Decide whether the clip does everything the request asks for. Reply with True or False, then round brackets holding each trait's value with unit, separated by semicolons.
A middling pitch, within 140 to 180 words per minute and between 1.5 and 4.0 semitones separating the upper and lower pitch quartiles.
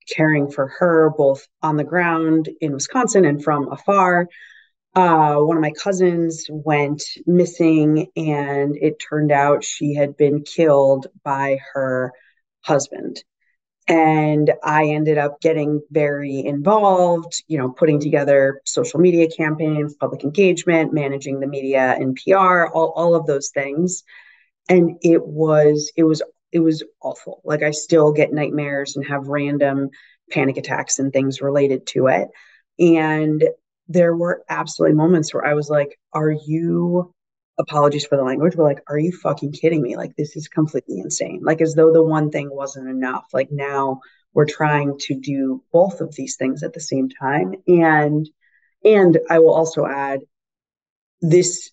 True (150 Hz; 155 wpm; 2.7 semitones)